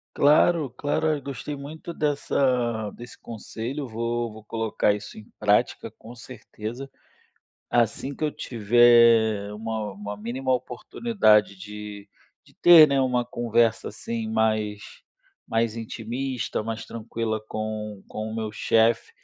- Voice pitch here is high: No, low, 115 Hz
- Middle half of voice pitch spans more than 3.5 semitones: No, average, 2.9 semitones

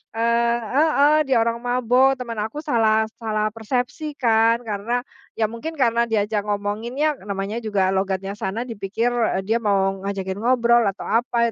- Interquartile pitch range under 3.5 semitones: Yes, average, 2.9 semitones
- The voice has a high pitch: Yes, high, 230 Hz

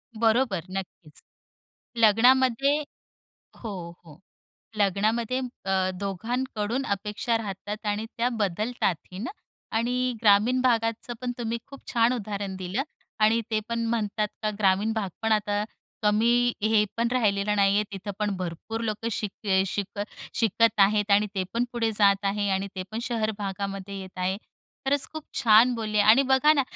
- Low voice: No, high, 215 Hz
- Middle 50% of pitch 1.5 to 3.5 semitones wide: Yes, average, 2.9 semitones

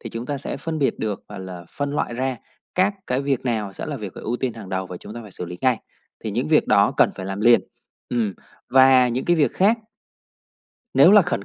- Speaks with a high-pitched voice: No, low, 120 Hz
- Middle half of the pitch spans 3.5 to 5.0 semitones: No, wide, 5.4 semitones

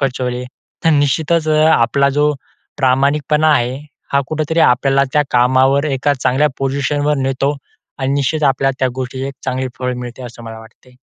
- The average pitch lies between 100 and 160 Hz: Yes, low, 135 Hz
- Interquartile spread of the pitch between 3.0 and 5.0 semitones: No, narrow, 2.4 semitones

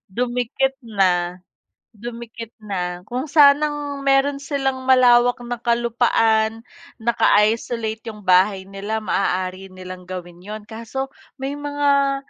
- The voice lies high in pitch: Yes, high, 235 Hz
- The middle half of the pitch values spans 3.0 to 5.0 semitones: Yes, average, 4.5 semitones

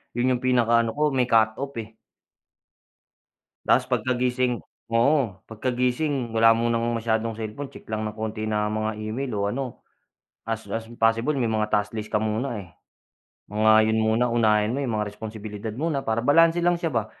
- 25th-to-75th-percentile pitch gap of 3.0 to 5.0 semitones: No, narrow, 2.6 semitones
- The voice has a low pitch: Yes, low, 115 Hz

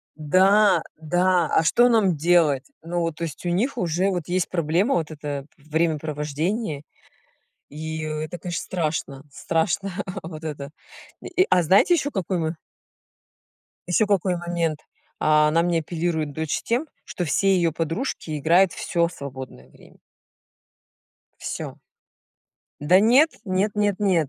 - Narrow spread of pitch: No, average, 3.3 semitones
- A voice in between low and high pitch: Yes, medium, 170 Hz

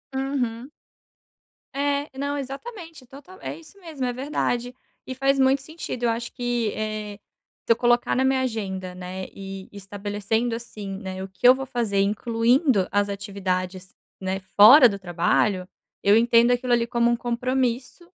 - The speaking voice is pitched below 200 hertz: No, high, 235 Hz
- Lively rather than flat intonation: No, average, 4.8 semitones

